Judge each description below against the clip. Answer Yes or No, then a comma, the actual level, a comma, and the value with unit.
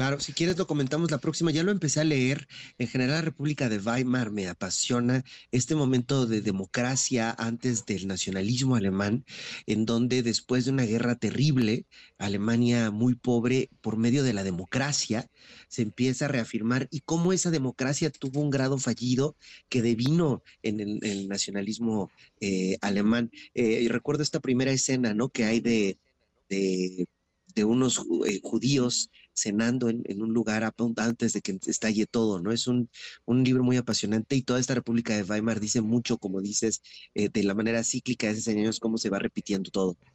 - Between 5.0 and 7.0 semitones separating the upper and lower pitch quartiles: No, average, 3.3 semitones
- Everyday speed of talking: Yes, average, 180 wpm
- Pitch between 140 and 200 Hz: No, low, 120 Hz